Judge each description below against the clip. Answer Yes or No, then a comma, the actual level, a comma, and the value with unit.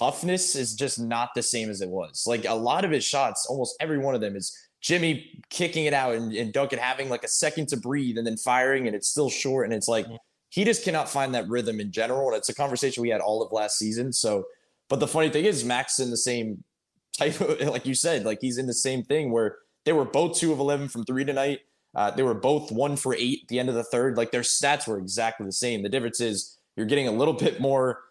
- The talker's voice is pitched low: Yes, low, 130 Hz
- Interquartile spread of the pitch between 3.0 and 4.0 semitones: Yes, average, 3.6 semitones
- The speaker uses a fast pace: Yes, fast, 260 wpm